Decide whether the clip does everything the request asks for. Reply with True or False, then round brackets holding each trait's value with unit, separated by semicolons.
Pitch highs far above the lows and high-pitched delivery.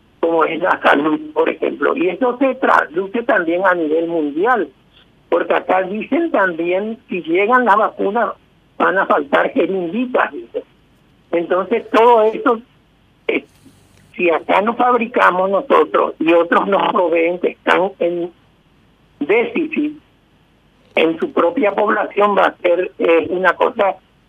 True (6.8 semitones; 210 Hz)